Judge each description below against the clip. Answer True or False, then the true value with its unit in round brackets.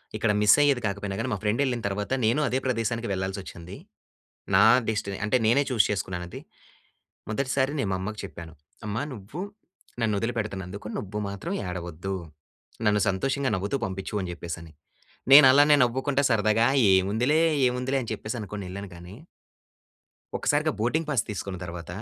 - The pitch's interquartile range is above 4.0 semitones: True (4.5 semitones)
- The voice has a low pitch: True (105 Hz)